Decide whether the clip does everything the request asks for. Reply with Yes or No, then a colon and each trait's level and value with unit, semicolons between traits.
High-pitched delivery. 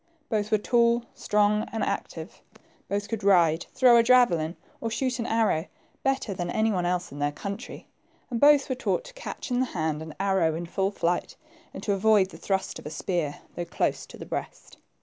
Yes: high, 200 Hz